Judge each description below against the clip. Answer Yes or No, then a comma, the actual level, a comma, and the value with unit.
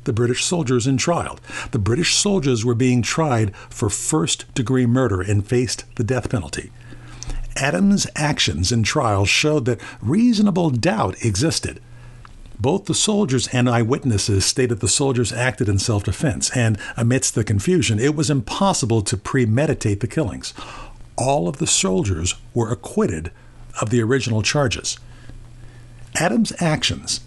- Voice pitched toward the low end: Yes, low, 125 Hz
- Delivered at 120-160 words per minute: Yes, average, 140 wpm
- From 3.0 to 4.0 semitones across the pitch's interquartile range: Yes, average, 3.4 semitones